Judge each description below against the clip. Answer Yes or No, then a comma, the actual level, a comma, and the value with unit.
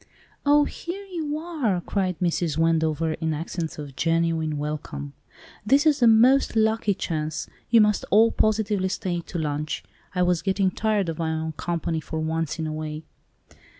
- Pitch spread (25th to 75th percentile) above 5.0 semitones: Yes, wide, 5.5 semitones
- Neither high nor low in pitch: Yes, medium, 175 Hz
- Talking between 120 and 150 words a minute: No, average, 165 wpm